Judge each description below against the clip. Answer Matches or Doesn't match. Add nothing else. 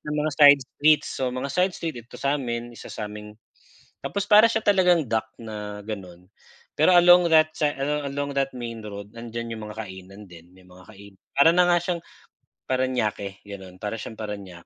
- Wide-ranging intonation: Matches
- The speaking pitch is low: Matches